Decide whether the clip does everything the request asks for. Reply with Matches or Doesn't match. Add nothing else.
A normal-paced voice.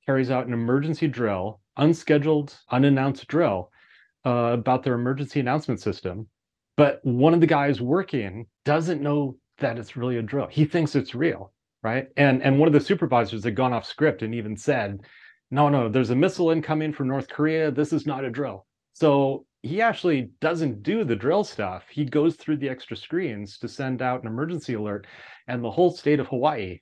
Matches